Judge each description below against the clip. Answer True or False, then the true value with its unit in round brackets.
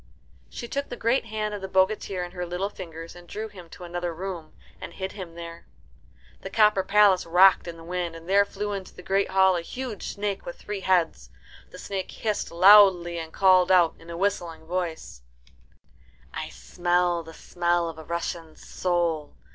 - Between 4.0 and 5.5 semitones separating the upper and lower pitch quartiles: False (2.7 semitones)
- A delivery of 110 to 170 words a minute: False (185 wpm)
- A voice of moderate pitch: True (180 Hz)